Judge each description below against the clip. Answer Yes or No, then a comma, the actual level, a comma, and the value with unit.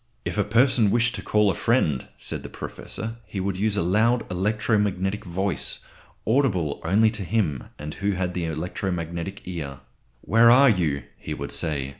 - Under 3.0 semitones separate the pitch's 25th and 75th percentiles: No, average, 4.2 semitones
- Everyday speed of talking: Yes, average, 180 wpm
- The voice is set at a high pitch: No, low, 100 Hz